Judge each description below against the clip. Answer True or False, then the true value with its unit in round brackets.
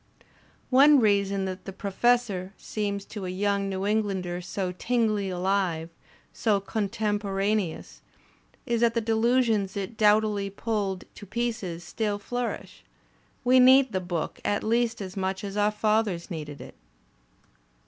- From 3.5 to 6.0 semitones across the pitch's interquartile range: False (2.8 semitones)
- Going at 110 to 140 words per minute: True (135 wpm)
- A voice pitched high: True (205 Hz)